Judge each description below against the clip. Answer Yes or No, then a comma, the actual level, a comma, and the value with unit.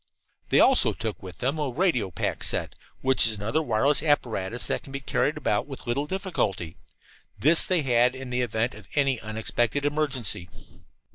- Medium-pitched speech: No, low, 125 Hz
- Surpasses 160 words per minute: Yes, average, 170 wpm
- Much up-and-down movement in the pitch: No, average, 4.8 semitones